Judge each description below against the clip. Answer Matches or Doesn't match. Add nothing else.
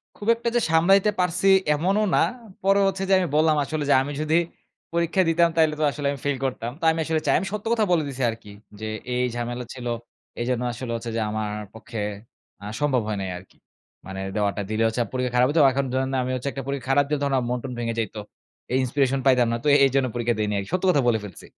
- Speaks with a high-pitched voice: Doesn't match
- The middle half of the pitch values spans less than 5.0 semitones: Doesn't match